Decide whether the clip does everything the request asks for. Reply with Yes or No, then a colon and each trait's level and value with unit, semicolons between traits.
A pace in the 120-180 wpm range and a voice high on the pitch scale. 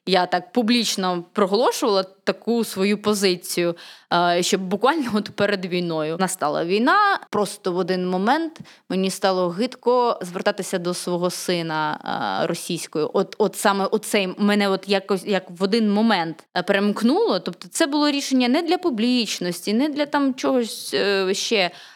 Yes: average, 140 wpm; high, 200 Hz